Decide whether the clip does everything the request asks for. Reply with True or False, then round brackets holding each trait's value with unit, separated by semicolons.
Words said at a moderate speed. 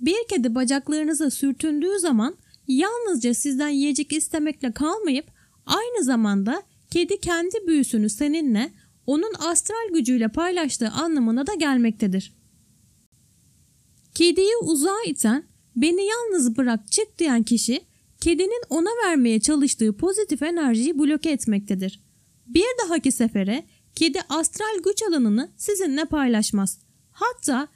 True (110 wpm)